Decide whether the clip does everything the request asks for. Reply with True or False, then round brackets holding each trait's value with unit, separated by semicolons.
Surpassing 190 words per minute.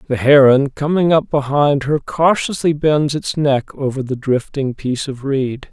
False (170 wpm)